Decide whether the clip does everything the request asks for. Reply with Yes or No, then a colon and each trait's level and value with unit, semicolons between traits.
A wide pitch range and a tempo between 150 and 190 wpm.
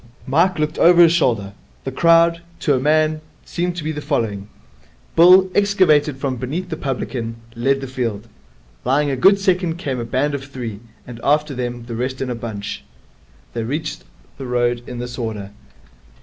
No: average, 5.0 semitones; average, 175 wpm